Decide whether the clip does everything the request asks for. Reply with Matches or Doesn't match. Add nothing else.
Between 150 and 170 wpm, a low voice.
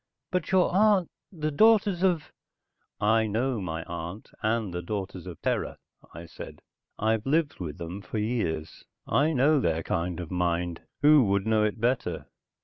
Matches